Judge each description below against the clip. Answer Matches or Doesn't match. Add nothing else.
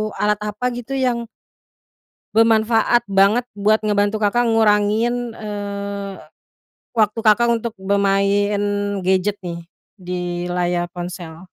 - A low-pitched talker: Doesn't match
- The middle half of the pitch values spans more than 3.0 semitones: Doesn't match